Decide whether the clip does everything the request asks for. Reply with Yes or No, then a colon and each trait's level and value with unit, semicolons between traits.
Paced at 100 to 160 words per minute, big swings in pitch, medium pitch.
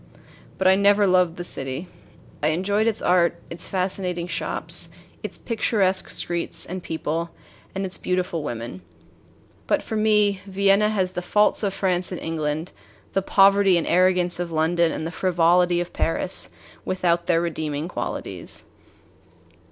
No: average, 145 wpm; narrow, 2.5 semitones; medium, 180 Hz